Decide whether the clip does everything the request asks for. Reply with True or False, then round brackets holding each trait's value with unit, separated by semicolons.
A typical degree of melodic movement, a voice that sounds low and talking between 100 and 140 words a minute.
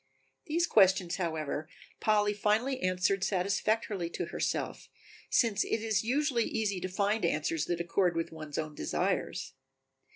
False (4.2 semitones; 195 Hz; 135 wpm)